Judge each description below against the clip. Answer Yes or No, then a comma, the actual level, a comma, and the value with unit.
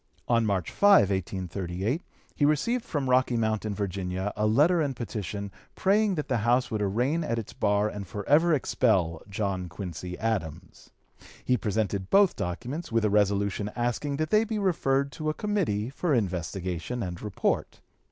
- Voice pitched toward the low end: Yes, low, 110 Hz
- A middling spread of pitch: No, wide, 6.3 semitones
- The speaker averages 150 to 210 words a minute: Yes, average, 160 wpm